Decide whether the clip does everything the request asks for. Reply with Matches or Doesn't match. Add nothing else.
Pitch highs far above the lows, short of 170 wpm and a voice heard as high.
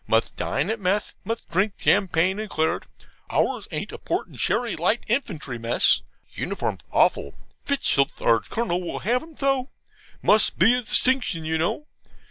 Matches